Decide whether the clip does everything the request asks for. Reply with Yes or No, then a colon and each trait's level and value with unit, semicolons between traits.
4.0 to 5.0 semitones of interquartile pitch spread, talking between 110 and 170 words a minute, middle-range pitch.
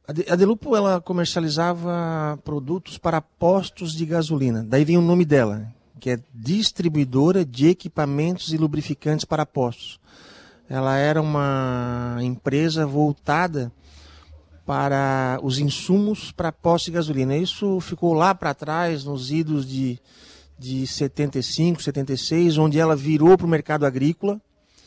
Yes: average, 4.3 semitones; average, 130 wpm; medium, 150 Hz